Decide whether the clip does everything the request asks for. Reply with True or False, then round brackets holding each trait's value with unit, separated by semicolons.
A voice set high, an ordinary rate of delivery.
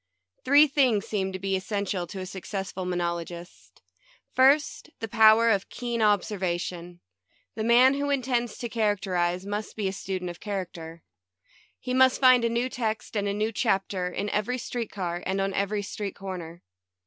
True (205 Hz; 170 wpm)